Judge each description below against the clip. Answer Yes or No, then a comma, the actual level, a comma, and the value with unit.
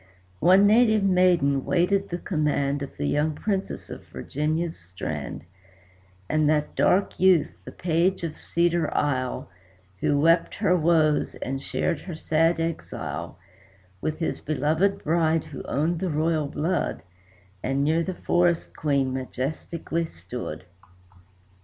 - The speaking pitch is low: No, medium, 160 Hz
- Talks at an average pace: No, slow, 130 wpm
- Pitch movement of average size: Yes, average, 3.1 semitones